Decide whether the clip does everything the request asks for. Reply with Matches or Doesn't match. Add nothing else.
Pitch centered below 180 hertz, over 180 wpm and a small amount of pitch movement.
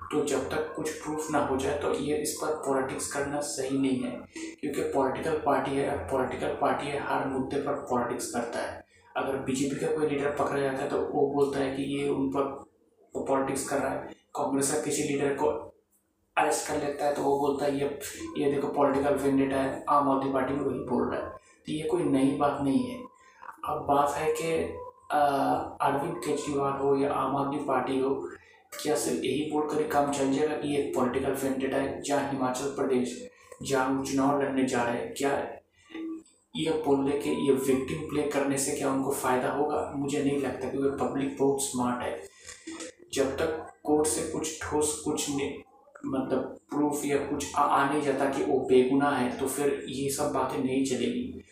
Matches